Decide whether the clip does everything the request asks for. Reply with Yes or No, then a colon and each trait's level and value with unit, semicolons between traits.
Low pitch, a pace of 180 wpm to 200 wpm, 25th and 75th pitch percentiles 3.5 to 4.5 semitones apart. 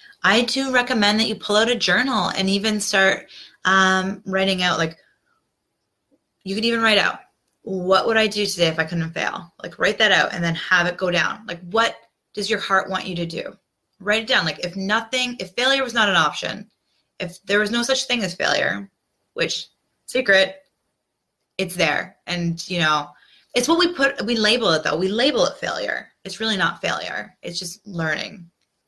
No: high, 195 Hz; average, 195 wpm; average, 3.8 semitones